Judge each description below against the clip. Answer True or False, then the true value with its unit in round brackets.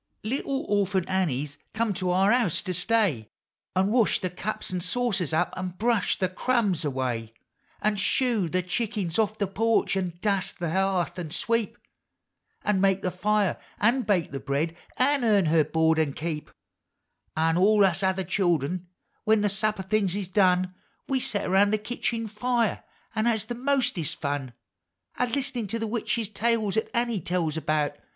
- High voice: True (195 Hz)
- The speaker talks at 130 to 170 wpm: False (180 wpm)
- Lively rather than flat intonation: False (4.2 semitones)